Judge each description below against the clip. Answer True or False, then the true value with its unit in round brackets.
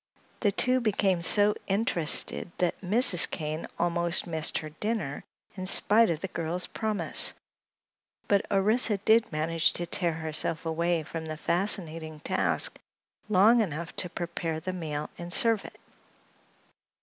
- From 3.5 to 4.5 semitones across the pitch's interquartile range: True (4.1 semitones)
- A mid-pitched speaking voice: True (175 Hz)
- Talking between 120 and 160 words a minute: True (135 wpm)